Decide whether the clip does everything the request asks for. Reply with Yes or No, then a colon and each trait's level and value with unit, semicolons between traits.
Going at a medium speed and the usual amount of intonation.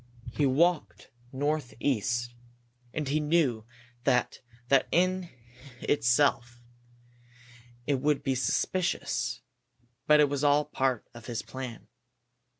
No: slow, 100 wpm; average, 3.6 semitones